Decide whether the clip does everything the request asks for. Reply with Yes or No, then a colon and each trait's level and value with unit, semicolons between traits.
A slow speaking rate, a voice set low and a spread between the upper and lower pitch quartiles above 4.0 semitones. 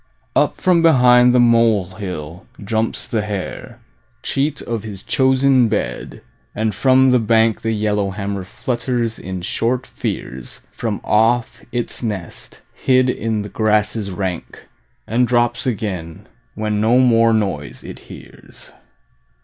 No: slow, 125 wpm; low, 110 Hz; average, 3.3 semitones